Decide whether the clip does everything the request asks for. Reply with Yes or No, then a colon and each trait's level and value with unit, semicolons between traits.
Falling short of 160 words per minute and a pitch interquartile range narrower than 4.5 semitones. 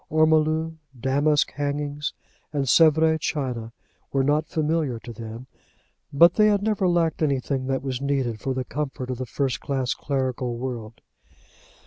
Yes: average, 145 wpm; average, 3.5 semitones